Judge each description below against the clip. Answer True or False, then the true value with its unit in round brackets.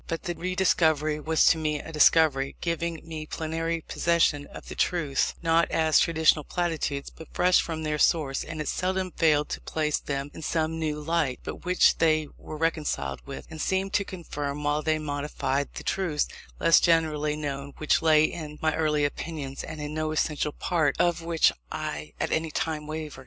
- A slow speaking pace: False (185 wpm)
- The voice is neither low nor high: True (155 Hz)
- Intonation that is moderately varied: False (1.8 semitones)